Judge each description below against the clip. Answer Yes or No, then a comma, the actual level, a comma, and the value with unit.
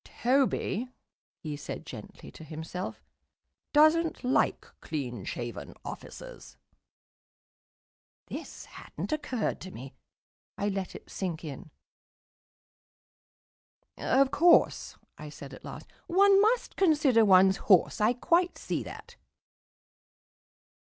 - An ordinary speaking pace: No, slow, 105 wpm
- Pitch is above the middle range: Yes, high, 205 Hz